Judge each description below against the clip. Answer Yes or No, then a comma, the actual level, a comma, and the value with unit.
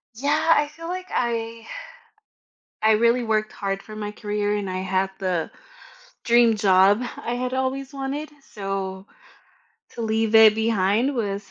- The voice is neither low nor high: No, high, 220 Hz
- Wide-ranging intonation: No, average, 3.8 semitones